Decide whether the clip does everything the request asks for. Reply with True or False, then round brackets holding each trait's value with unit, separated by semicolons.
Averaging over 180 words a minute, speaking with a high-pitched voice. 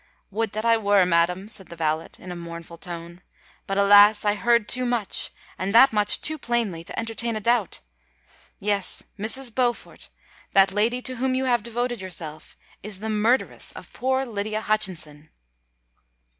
False (155 wpm; 210 Hz)